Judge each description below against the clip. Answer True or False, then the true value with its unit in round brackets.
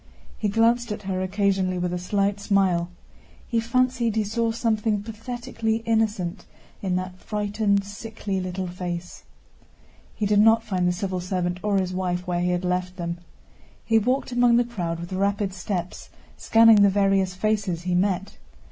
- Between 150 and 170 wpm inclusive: True (165 wpm)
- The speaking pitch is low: False (200 Hz)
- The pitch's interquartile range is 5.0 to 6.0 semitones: False (3.4 semitones)